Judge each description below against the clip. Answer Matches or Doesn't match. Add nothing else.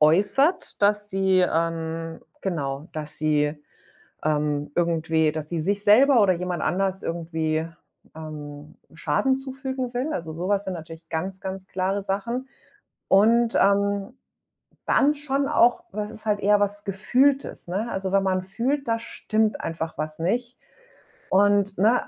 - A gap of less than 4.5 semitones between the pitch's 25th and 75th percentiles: Doesn't match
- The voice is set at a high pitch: Matches